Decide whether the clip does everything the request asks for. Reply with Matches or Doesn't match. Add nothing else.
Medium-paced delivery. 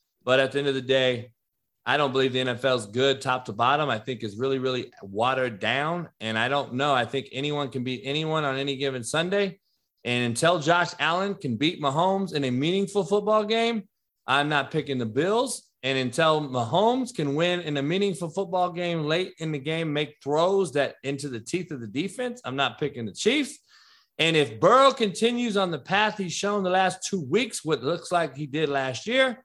Doesn't match